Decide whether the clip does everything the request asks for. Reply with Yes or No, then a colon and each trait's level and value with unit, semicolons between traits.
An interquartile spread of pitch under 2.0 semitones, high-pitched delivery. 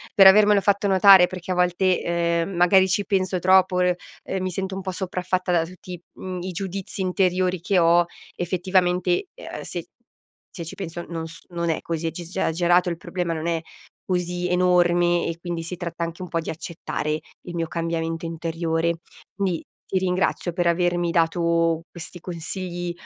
No: narrow, 1.6 semitones; medium, 175 Hz